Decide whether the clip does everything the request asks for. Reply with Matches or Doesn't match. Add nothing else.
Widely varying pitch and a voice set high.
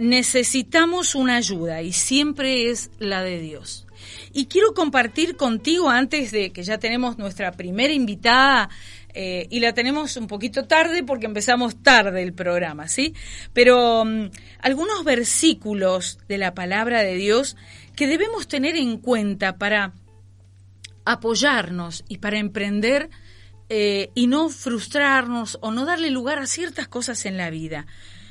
Matches